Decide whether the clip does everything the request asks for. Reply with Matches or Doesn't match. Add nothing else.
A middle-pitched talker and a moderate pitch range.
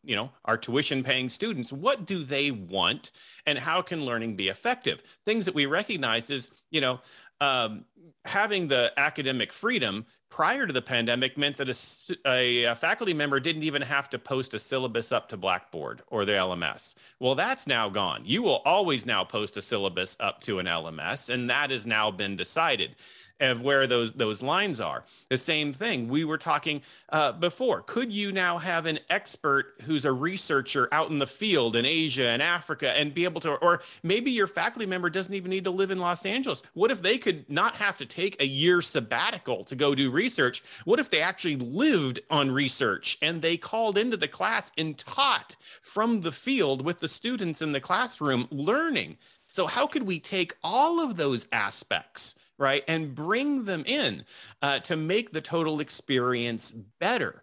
Doesn't match